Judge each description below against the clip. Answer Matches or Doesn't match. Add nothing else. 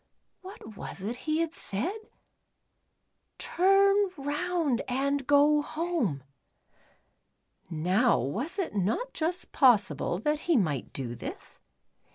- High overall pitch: Matches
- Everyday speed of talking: Doesn't match